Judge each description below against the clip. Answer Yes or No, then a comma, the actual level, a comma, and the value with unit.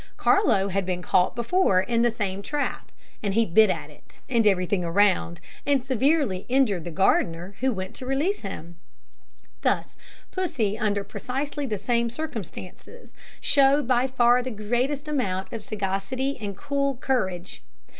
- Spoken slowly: No, average, 155 wpm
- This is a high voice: Yes, high, 225 Hz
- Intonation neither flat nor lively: No, wide, 5.8 semitones